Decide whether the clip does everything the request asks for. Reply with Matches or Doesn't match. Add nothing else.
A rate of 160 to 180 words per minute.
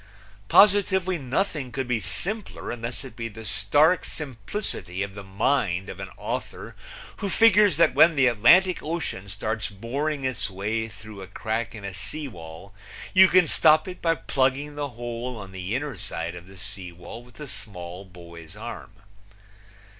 Matches